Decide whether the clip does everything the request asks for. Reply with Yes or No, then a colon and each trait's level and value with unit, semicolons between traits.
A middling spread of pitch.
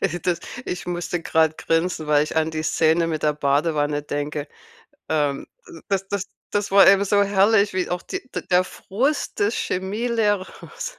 Yes: average, 4.3 semitones